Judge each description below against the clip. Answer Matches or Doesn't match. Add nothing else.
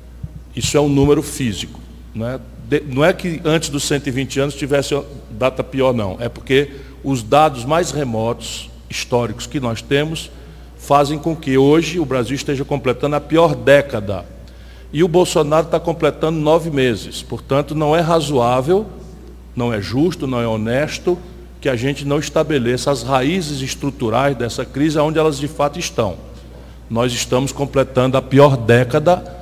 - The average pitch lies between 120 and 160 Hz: Matches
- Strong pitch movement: Doesn't match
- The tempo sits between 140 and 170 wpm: Matches